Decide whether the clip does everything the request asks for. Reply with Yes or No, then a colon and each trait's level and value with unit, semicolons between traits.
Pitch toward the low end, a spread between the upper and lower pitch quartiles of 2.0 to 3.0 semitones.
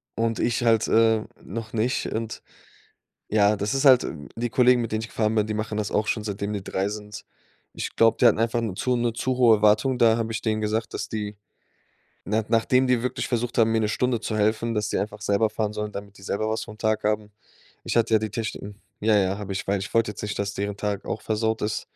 No: low, 110 Hz; narrow, 1.6 semitones